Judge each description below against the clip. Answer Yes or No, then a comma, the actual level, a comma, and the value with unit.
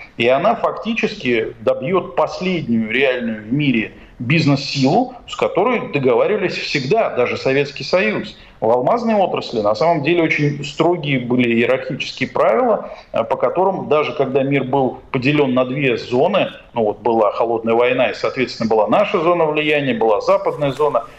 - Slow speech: No, average, 145 wpm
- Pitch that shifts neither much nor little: Yes, average, 4.9 semitones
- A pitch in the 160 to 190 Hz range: No, medium, 140 Hz